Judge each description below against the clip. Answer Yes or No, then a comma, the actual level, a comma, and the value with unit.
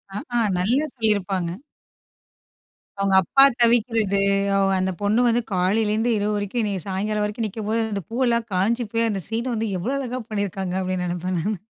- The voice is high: Yes, high, 210 Hz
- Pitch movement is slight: No, average, 3.1 semitones